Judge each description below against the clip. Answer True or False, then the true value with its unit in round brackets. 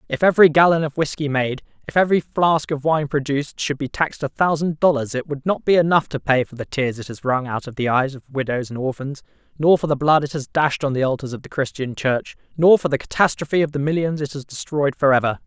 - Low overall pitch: False (145 Hz)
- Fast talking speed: True (250 wpm)